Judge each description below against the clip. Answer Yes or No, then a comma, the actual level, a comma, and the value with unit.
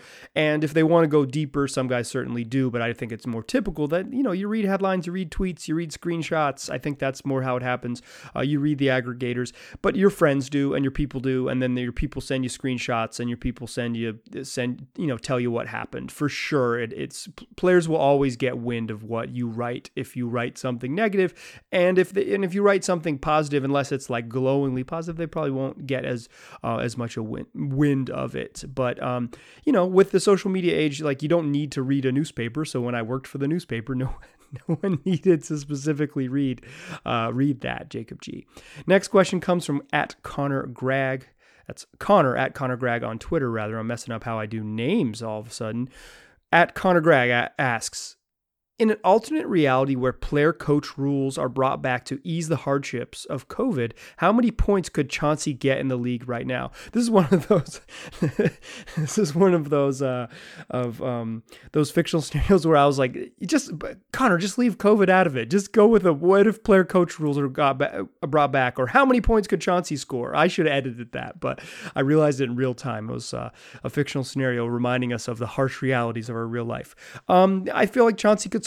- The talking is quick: Yes, fast, 225 wpm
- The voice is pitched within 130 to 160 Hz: Yes, medium, 140 Hz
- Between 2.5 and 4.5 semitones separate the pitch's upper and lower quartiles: No, average, 5.3 semitones